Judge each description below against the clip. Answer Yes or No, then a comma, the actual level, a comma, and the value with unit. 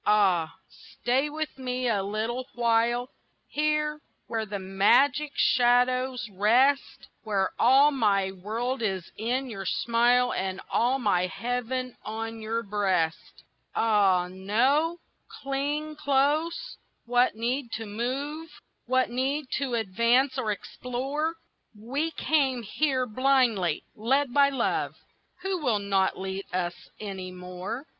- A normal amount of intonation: Yes, average, 4.7 semitones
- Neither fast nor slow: No, slow, 120 wpm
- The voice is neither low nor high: No, high, 240 Hz